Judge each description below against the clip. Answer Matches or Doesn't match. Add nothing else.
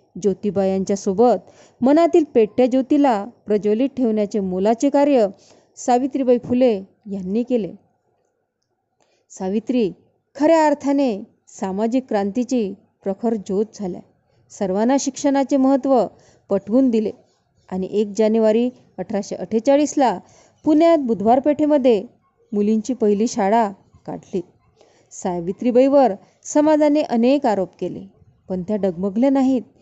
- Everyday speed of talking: Matches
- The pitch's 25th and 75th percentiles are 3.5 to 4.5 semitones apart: Doesn't match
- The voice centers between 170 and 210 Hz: Doesn't match